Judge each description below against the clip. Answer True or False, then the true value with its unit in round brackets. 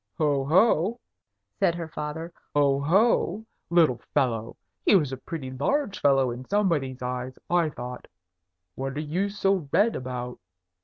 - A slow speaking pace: False (145 wpm)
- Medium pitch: True (150 Hz)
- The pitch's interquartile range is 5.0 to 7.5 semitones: True (5.6 semitones)